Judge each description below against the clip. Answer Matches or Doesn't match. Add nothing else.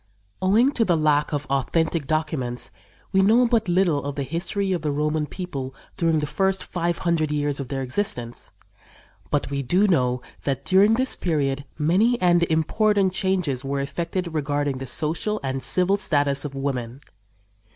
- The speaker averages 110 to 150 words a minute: Doesn't match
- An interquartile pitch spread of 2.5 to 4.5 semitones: Doesn't match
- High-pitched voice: Doesn't match